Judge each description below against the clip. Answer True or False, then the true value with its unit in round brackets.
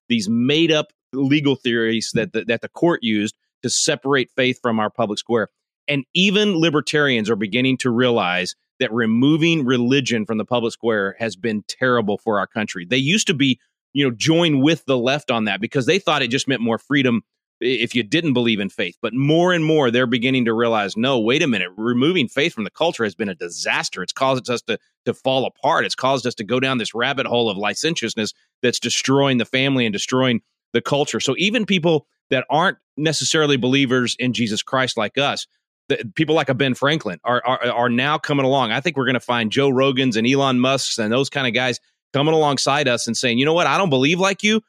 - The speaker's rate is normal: False (220 wpm)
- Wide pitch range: False (3.5 semitones)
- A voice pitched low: True (130 Hz)